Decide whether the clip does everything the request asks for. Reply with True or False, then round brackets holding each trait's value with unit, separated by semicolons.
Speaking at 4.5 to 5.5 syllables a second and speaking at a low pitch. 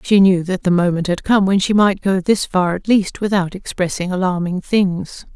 False (4.8 syllables/s; 190 Hz)